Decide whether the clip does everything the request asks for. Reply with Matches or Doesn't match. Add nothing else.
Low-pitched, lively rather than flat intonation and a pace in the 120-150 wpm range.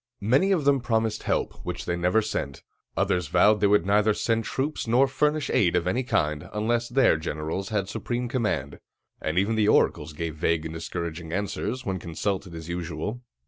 Doesn't match